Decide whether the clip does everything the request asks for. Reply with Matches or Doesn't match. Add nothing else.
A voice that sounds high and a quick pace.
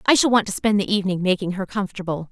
Matches